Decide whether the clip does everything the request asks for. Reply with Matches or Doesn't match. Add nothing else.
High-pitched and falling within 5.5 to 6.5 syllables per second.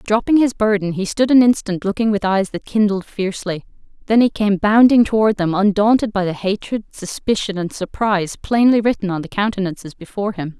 Matches